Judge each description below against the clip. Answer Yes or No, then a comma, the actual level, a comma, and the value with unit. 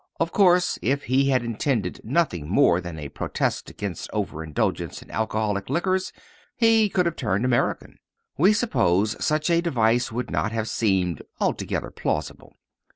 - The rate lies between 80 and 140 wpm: No, average, 150 wpm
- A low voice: Yes, low, 120 Hz